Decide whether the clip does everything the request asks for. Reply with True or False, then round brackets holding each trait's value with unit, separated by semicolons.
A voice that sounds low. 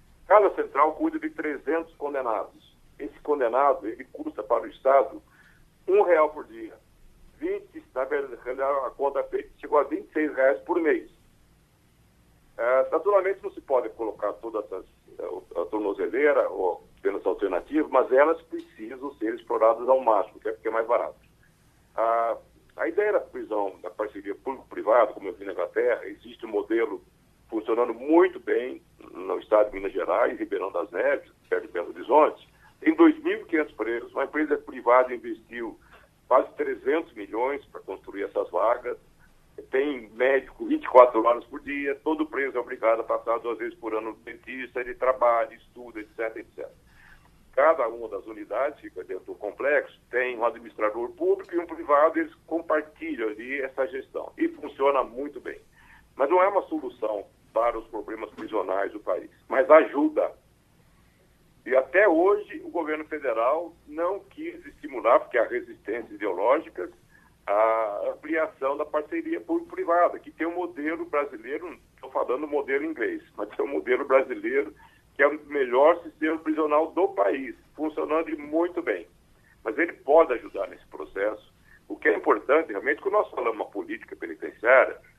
False (340 Hz)